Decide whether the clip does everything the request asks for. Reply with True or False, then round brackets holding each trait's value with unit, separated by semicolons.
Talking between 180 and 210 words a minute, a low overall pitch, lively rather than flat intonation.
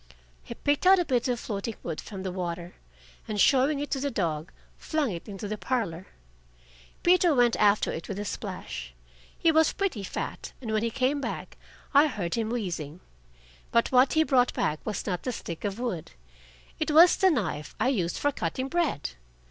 False (190 wpm; 230 Hz; 7.5 semitones)